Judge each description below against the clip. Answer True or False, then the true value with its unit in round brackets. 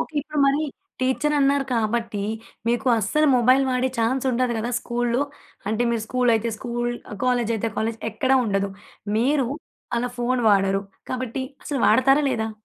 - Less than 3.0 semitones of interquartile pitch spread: True (2.6 semitones)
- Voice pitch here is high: True (245 Hz)